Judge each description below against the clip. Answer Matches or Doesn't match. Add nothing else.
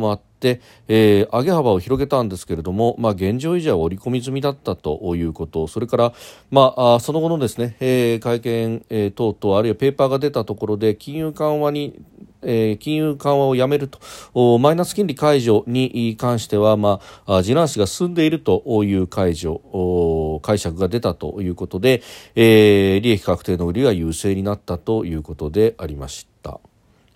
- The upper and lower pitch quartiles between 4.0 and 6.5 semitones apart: Matches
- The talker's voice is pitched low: Matches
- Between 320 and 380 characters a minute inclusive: Matches